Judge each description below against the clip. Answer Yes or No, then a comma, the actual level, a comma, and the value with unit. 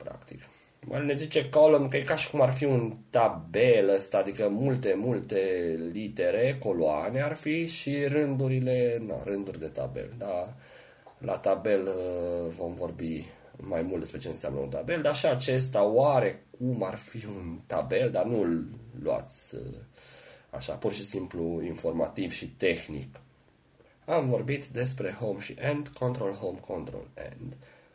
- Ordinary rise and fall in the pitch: No, wide, 8.2 semitones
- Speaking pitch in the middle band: No, low, 125 Hz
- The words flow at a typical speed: Yes, average, 145 wpm